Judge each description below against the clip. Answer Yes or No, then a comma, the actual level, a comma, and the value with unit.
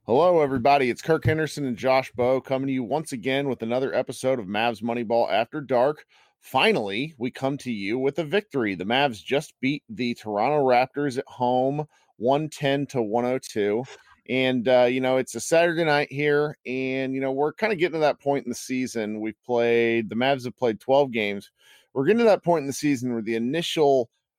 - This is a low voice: Yes, low, 130 Hz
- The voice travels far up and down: No, average, 2.9 semitones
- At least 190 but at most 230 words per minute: Yes, average, 200 wpm